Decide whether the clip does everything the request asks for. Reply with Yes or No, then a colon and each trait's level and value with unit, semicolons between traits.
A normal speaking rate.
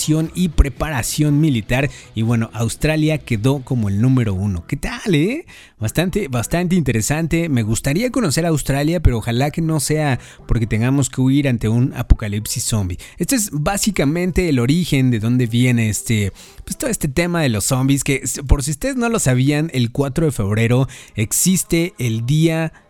Yes: average, 170 wpm